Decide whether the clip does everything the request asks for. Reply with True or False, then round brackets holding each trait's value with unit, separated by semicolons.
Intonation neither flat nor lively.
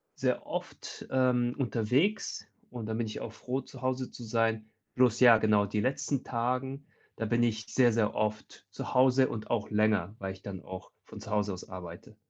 True (3.1 semitones)